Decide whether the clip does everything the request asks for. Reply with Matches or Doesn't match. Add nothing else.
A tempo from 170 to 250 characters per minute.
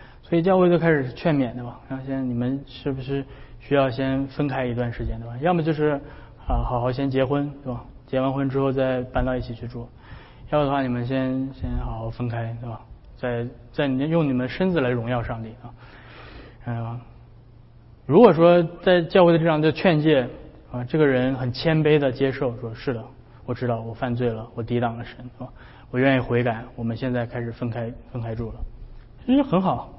Doesn't match